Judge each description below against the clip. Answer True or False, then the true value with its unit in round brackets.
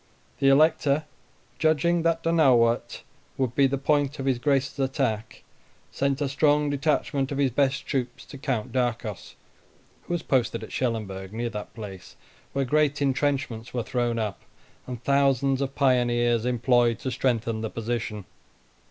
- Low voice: True (130 Hz)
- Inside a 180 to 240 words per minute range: False (150 wpm)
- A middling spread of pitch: True (3.0 semitones)